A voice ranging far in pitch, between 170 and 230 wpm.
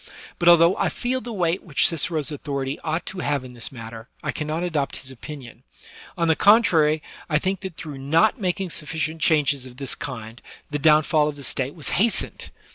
No: average, 3.8 semitones; average, 200 wpm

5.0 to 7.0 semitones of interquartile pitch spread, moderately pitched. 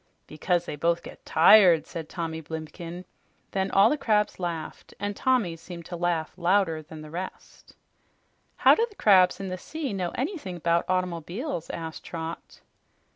No: average, 3.0 semitones; medium, 175 Hz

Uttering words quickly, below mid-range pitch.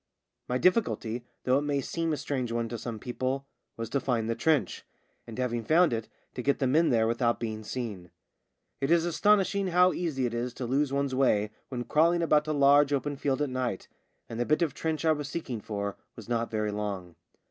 Yes: fast, 220 wpm; low, 130 Hz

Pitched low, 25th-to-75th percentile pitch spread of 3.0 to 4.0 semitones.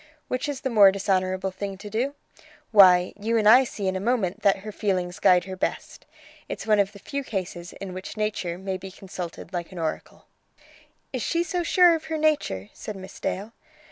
No: high, 200 Hz; average, 3.6 semitones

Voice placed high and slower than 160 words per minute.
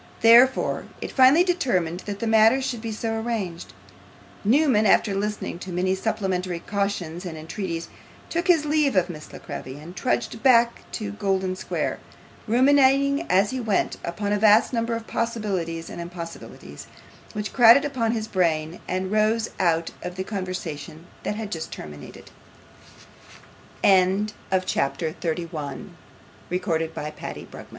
Yes: high, 205 Hz; average, 140 wpm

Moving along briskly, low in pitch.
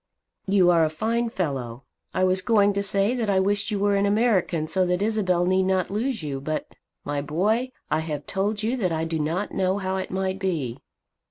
No: fast, 210 wpm; high, 190 Hz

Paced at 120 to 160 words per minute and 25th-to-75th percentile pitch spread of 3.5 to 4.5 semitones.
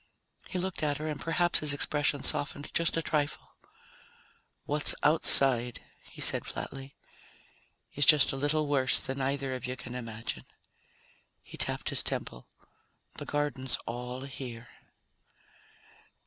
No: slow, 135 wpm; narrow, 2.5 semitones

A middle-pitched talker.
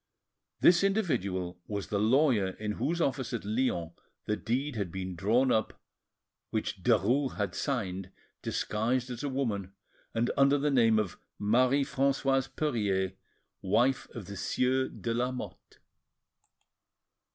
No: low, 115 Hz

